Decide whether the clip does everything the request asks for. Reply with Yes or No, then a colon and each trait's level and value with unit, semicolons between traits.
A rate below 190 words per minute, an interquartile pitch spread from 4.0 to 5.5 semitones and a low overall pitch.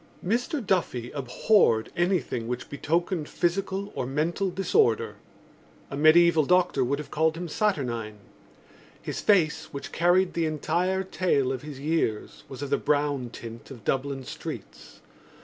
No: average, 140 wpm; average, 5.2 semitones; medium, 155 Hz